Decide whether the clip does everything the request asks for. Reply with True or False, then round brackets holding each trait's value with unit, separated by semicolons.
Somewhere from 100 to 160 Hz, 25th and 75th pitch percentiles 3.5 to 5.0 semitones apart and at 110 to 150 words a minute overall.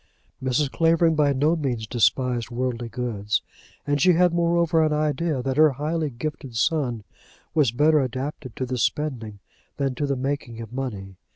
False (135 Hz; 4.1 semitones; 165 wpm)